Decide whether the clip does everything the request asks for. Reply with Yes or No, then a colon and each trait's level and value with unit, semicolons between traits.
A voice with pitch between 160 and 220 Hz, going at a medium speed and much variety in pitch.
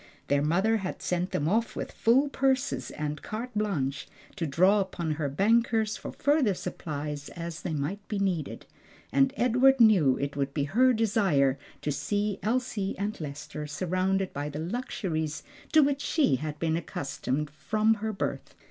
Yes: medium, 185 Hz; average, 165 wpm; wide, 6.8 semitones